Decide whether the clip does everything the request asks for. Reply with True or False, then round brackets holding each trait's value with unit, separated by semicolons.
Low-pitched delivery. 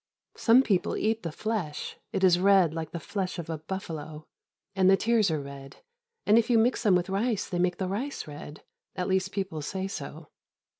False (185 Hz)